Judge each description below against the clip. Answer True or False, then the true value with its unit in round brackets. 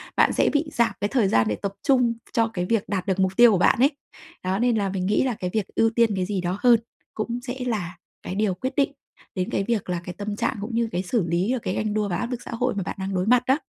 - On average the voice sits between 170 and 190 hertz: False (210 Hz)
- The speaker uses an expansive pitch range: False (4.2 semitones)